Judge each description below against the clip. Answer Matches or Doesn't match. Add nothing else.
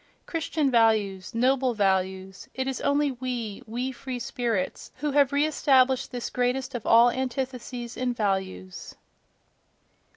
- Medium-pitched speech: Doesn't match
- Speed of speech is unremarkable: Doesn't match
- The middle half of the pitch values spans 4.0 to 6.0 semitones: Doesn't match